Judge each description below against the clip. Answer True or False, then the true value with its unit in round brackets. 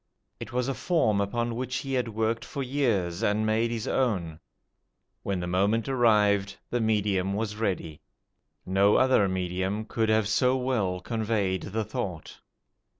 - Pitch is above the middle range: False (110 Hz)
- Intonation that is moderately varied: True (3.4 semitones)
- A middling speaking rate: True (150 wpm)